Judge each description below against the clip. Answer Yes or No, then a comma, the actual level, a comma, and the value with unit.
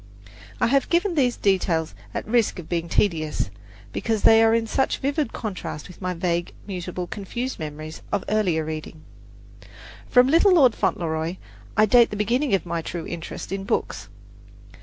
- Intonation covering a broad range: Yes, wide, 6.0 semitones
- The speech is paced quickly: No, average, 170 wpm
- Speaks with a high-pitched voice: Yes, high, 195 Hz